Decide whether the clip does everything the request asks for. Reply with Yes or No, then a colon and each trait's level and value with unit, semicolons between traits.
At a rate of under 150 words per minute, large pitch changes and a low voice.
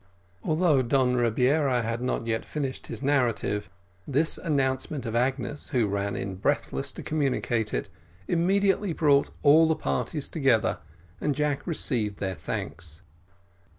No: slow, 135 wpm; average, 4.8 semitones; low, 130 Hz